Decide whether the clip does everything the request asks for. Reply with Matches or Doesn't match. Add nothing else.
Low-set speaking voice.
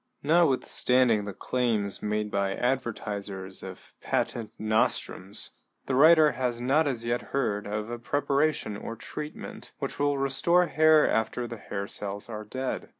Matches